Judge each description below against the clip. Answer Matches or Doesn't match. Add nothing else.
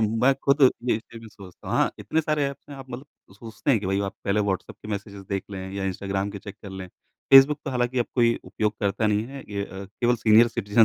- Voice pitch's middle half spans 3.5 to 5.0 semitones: Matches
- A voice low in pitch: Matches